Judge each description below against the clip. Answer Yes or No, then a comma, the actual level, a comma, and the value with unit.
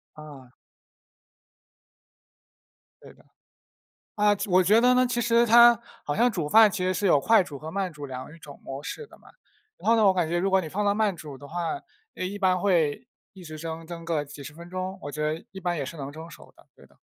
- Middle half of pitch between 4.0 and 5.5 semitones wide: Yes, average, 5.2 semitones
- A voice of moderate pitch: Yes, medium, 180 Hz